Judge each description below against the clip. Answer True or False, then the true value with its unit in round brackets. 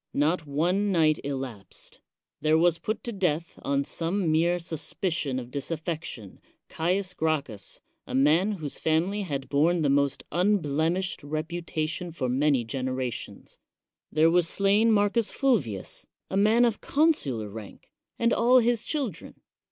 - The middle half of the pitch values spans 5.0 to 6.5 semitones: True (5.5 semitones)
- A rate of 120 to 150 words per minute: True (135 wpm)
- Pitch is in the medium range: True (160 Hz)